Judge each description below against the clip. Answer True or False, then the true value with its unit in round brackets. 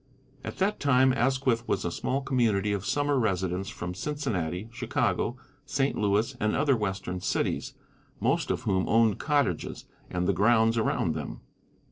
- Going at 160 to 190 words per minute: False (150 wpm)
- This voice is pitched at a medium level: False (110 Hz)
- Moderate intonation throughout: False (5.7 semitones)